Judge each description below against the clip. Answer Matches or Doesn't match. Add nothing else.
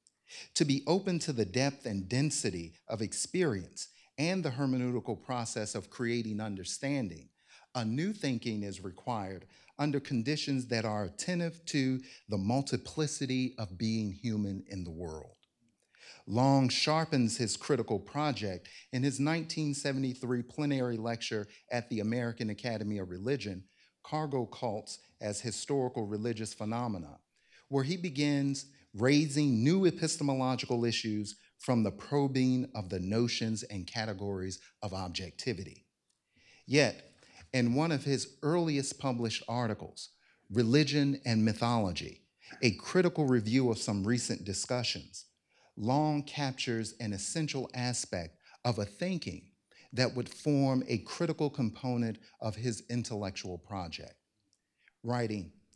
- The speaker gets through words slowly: Matches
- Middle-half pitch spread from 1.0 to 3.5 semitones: Doesn't match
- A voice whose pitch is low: Matches